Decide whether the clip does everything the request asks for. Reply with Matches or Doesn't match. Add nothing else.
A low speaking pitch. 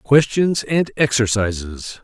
Matches